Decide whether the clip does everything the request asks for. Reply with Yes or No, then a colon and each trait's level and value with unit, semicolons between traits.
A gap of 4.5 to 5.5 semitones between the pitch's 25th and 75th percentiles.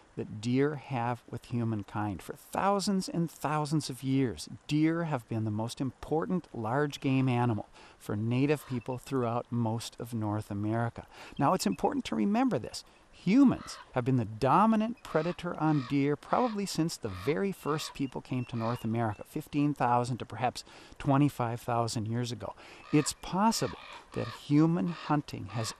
Yes: average, 4.8 semitones